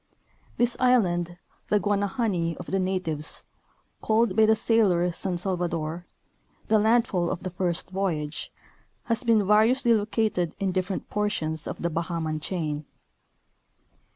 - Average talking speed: No, slow, 125 wpm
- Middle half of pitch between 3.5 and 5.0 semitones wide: Yes, average, 4.0 semitones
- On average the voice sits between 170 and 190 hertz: Yes, medium, 185 Hz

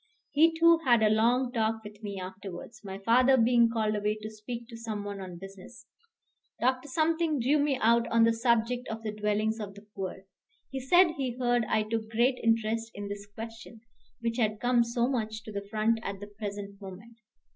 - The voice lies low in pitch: No, high, 225 Hz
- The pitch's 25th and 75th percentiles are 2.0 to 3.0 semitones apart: Yes, narrow, 2.5 semitones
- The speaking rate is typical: Yes, average, 195 wpm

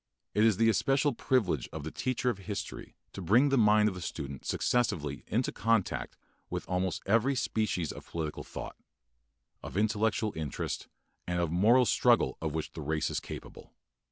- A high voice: No, low, 105 Hz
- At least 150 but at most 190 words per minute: Yes, average, 170 wpm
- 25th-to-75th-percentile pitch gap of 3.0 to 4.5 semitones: No, average, 5.3 semitones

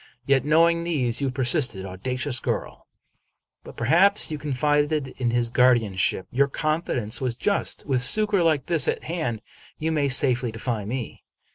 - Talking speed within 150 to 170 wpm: Yes, average, 155 wpm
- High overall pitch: No, low, 135 Hz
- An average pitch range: Yes, average, 4.3 semitones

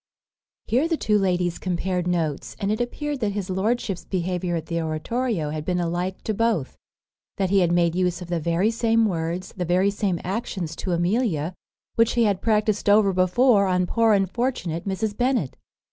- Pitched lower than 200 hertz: Yes, high, 190 Hz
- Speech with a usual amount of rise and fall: Yes, average, 4.0 semitones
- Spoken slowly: No, average, 180 wpm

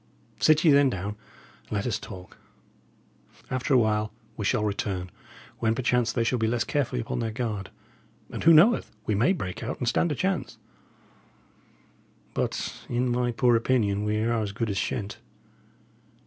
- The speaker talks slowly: No, average, 170 wpm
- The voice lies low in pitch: Yes, low, 115 Hz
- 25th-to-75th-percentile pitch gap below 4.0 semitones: Yes, average, 3.2 semitones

